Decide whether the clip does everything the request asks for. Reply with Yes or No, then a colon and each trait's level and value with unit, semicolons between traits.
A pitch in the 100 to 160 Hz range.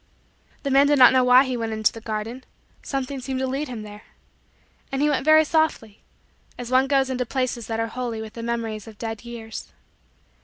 No: very high, 250 Hz